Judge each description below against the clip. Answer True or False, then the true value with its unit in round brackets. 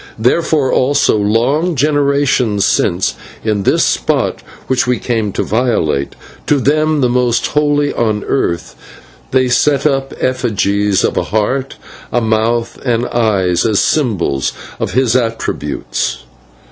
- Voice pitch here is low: True (120 Hz)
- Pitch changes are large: False (4.5 semitones)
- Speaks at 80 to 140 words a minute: True (135 wpm)